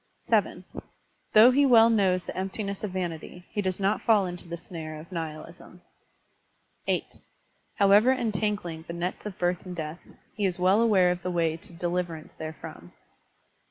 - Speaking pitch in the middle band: Yes, medium, 180 Hz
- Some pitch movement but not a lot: Yes, average, 3.3 semitones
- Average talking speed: Yes, average, 165 wpm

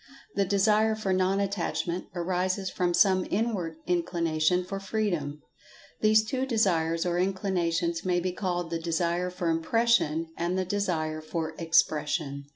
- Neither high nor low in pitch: Yes, medium, 180 Hz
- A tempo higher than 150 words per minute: No, average, 145 wpm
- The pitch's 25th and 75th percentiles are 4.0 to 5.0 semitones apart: No, average, 2.9 semitones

